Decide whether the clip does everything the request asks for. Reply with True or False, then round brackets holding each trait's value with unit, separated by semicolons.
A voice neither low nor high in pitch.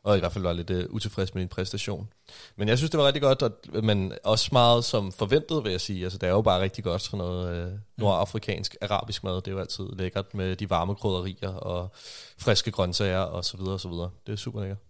False (100 Hz)